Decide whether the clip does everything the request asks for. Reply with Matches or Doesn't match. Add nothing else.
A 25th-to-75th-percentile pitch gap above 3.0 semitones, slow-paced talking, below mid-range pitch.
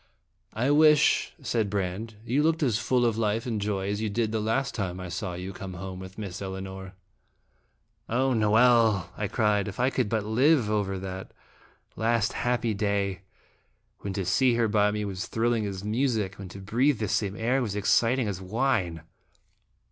Doesn't match